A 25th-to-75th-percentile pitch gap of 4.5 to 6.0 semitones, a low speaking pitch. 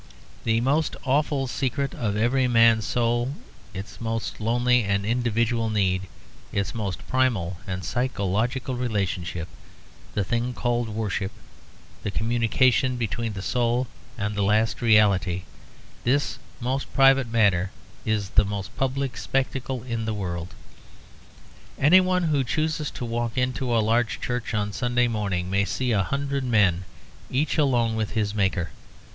No: average, 3.8 semitones; low, 115 Hz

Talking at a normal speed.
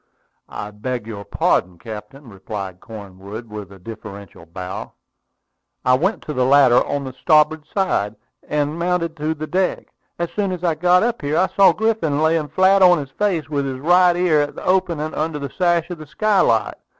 Yes: average, 185 wpm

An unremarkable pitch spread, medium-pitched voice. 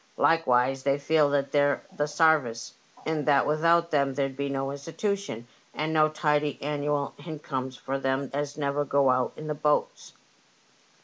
No: narrow, 2.1 semitones; medium, 145 Hz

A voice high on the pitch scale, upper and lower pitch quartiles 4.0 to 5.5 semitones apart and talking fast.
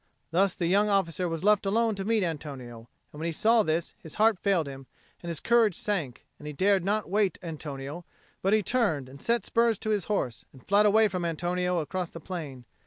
No: medium, 180 Hz; average, 5.0 semitones; fast, 215 wpm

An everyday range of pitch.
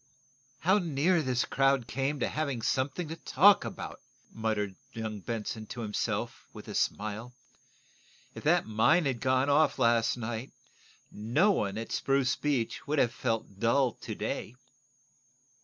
Yes: average, 4.1 semitones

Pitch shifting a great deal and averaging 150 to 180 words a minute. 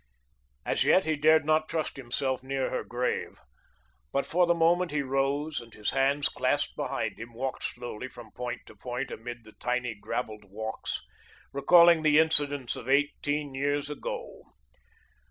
No: average, 3.9 semitones; average, 155 wpm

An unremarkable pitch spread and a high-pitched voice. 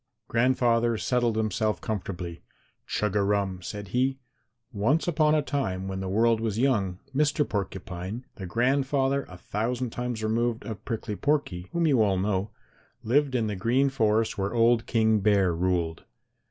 No: average, 4.4 semitones; low, 110 Hz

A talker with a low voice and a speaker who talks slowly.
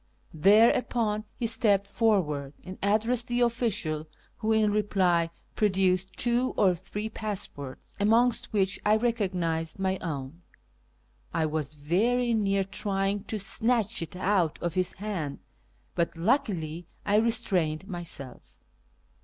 No: high, 195 Hz; slow, 125 wpm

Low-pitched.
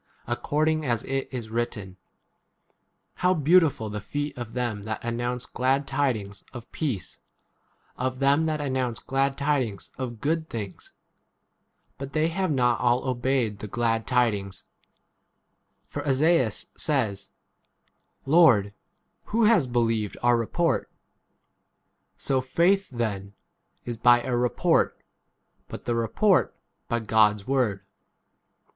Yes: low, 125 Hz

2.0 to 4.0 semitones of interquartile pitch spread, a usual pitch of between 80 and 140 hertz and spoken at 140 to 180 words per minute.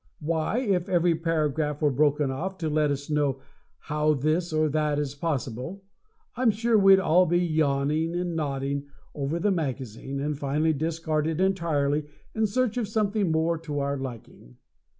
No: average, 3.6 semitones; medium, 155 Hz; average, 165 wpm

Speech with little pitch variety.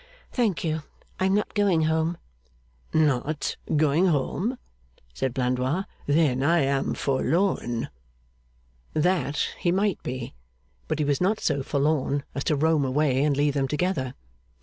No: average, 3.9 semitones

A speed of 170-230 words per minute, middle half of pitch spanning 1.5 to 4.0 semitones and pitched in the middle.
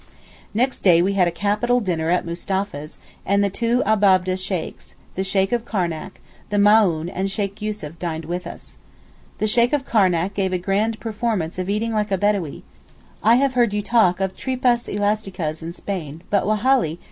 No: average, 180 wpm; average, 3.3 semitones; high, 200 Hz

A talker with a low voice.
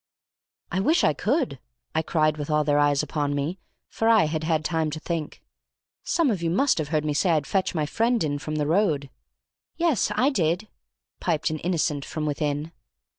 No: medium, 155 Hz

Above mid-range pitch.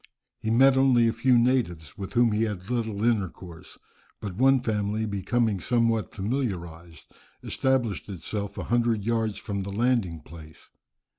No: low, 110 Hz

